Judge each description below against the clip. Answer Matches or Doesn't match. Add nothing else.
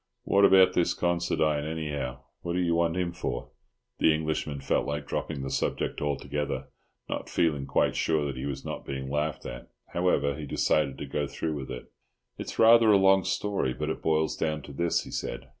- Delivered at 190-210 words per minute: Matches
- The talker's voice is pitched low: Matches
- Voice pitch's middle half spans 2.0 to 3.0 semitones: Doesn't match